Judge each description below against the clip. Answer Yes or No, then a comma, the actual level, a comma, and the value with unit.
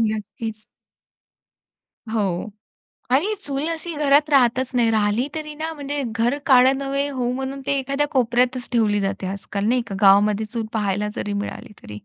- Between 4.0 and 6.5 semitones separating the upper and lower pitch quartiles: Yes, average, 4.7 semitones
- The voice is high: Yes, high, 245 Hz